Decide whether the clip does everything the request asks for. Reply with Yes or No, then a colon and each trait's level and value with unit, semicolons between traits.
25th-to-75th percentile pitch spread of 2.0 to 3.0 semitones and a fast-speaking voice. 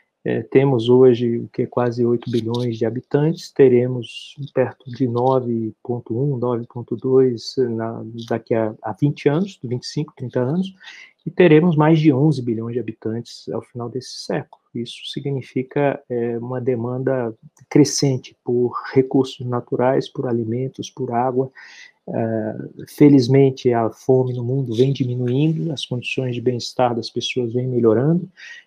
No: narrow, 2.6 semitones; average, 135 wpm